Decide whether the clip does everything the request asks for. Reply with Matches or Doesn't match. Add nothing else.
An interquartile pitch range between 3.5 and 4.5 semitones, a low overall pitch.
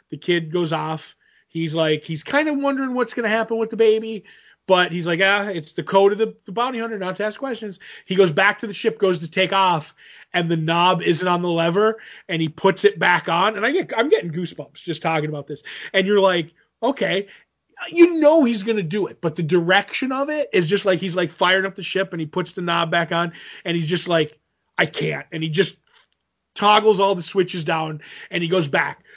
Doesn't match